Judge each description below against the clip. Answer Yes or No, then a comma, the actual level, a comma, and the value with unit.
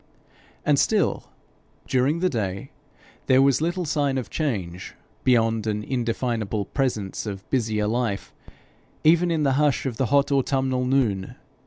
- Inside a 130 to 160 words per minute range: Yes, average, 140 wpm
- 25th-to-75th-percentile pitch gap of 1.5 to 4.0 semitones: No, average, 4.4 semitones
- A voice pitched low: Yes, low, 125 Hz